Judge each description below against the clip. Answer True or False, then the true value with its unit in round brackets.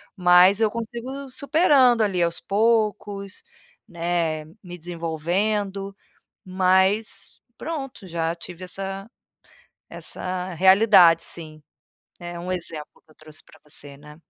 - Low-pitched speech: False (185 Hz)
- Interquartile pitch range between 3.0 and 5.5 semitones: True (3.8 semitones)